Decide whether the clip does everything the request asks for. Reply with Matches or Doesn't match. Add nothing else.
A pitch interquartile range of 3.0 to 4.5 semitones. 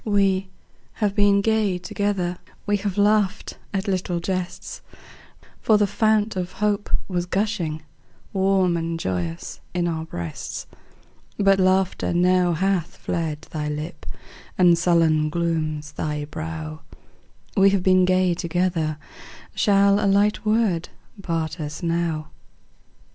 Matches